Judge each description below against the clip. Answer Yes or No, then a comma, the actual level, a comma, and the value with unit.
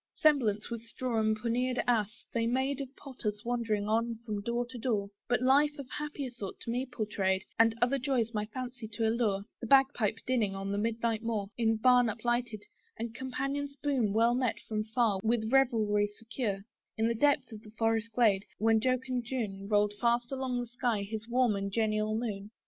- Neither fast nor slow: Yes, average, 185 wpm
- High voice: Yes, high, 230 Hz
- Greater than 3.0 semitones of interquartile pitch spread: No, average, 2.7 semitones